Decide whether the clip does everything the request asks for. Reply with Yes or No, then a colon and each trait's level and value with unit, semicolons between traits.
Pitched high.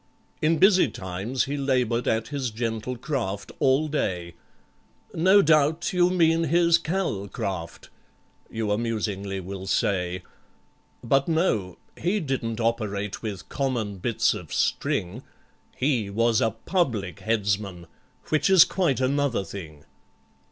No: low, 115 Hz